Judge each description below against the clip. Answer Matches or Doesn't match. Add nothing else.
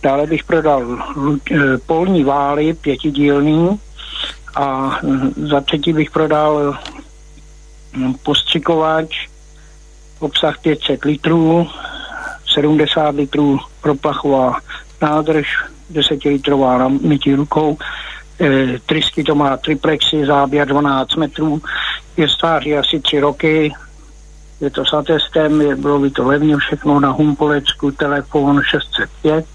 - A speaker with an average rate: Doesn't match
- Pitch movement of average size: Doesn't match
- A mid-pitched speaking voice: Matches